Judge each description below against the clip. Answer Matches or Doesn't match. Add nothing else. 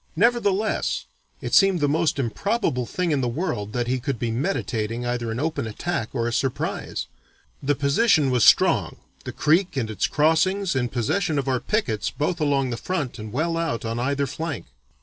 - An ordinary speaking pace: Matches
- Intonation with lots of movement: Matches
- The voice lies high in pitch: Doesn't match